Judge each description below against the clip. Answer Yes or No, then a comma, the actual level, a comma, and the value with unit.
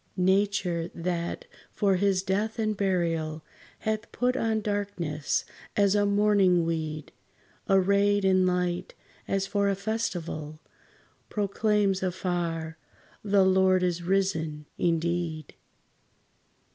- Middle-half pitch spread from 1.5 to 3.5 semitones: Yes, average, 3.0 semitones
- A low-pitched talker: No, high, 190 Hz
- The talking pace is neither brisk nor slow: No, slow, 105 wpm